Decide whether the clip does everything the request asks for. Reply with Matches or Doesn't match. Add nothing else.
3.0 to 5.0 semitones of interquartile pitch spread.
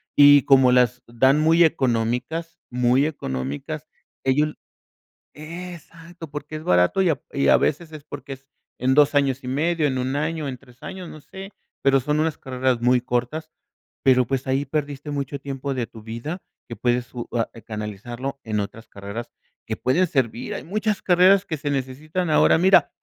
Matches